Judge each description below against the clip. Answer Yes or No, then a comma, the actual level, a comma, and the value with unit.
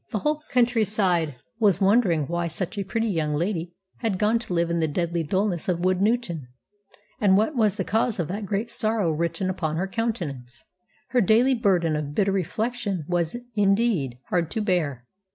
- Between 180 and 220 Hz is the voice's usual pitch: Yes, high, 190 Hz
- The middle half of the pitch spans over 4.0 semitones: Yes, average, 4.5 semitones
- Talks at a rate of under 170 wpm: No, average, 180 wpm